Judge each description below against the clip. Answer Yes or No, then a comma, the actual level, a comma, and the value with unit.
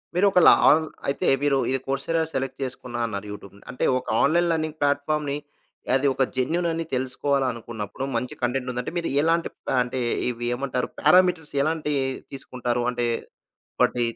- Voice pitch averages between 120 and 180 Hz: Yes, low, 135 Hz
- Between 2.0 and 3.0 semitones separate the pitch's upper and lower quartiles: No, average, 4.2 semitones